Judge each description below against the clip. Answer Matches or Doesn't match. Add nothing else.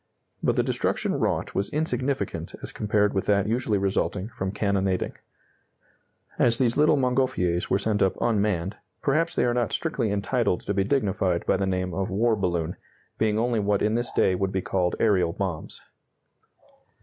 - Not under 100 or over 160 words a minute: Doesn't match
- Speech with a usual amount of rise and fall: Matches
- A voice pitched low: Matches